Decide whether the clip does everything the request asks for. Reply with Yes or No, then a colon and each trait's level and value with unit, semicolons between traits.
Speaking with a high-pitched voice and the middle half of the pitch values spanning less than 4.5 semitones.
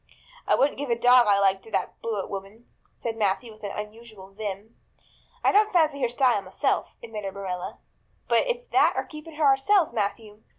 No: high, 225 Hz; average, 5.3 semitones